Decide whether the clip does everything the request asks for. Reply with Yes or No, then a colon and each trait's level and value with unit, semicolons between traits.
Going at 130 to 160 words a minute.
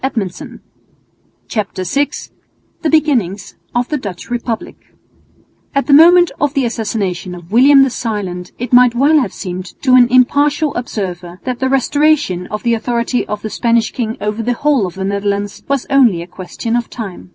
No: average, 170 wpm